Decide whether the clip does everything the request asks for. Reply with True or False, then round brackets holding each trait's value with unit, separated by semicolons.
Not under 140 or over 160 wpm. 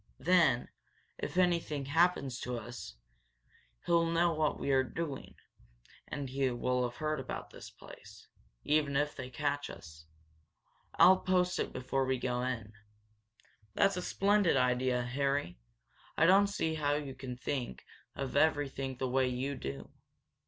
True (145 wpm)